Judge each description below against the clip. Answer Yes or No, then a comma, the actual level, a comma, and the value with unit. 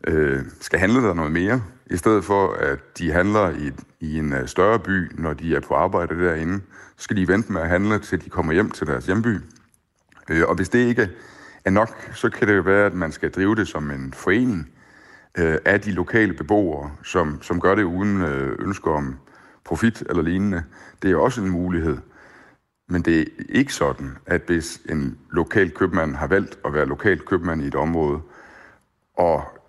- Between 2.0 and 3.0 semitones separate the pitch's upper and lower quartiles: No, average, 4.0 semitones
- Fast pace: No, average, 190 wpm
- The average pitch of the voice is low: Yes, very low, 90 Hz